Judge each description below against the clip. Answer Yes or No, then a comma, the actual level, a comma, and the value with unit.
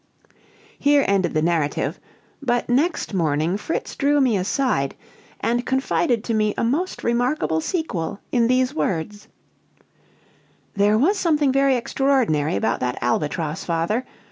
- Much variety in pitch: Yes, wide, 8.3 semitones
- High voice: Yes, high, 230 Hz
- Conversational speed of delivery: No, slow, 130 wpm